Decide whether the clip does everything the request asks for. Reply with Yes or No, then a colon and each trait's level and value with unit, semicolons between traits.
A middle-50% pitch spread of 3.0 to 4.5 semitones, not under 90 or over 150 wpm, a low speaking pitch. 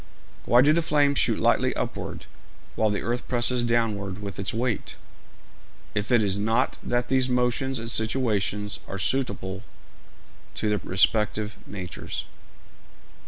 Yes: average, 3.4 semitones; slow, 135 wpm; low, 110 Hz